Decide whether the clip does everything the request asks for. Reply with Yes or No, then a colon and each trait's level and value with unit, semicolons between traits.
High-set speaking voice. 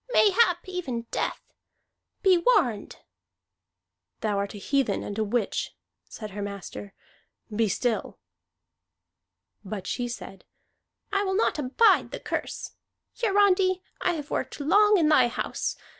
Yes: very high, 290 Hz